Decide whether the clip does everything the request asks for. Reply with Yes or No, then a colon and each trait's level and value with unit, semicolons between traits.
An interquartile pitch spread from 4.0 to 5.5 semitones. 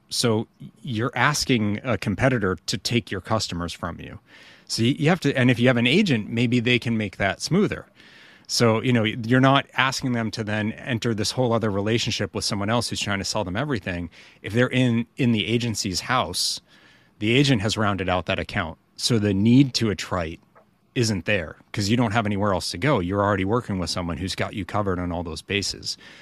No: average, 3.6 semitones